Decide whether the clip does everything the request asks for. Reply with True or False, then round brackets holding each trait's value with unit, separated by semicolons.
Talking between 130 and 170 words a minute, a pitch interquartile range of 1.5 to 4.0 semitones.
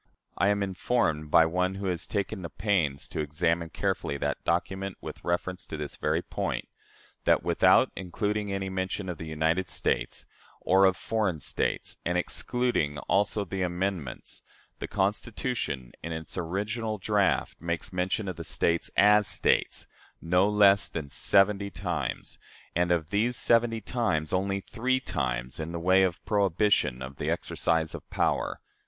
True (160 wpm; 3.7 semitones)